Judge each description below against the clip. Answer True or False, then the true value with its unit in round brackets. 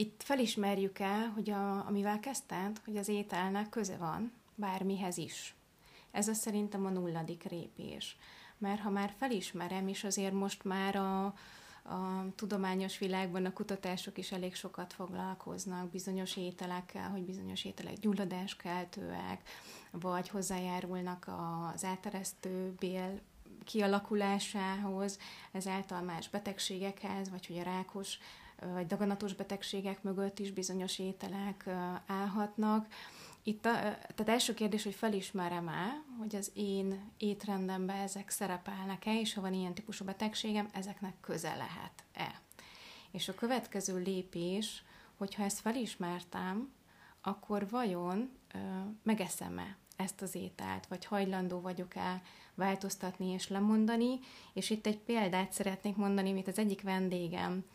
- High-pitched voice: True (195 Hz)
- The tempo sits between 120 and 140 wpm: True (125 wpm)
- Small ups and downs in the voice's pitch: True (1.9 semitones)